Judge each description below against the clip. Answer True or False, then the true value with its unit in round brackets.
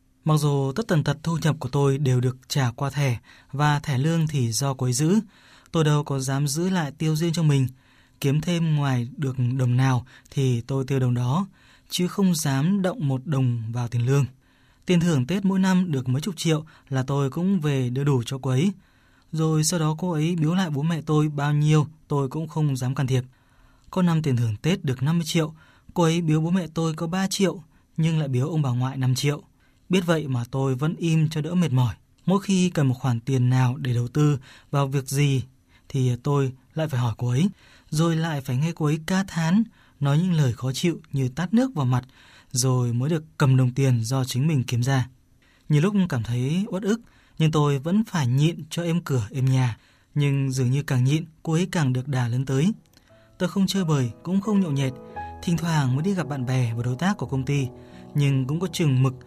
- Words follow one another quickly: False (230 wpm)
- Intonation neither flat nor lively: True (4.3 semitones)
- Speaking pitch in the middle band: True (145 Hz)